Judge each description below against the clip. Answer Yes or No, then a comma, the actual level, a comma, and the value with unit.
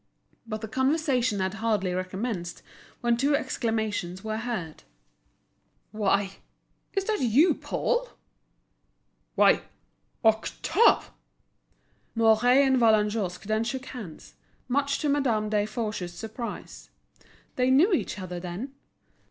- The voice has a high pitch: Yes, high, 225 Hz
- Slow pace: Yes, slow, 105 wpm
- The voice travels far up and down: No, average, 4.2 semitones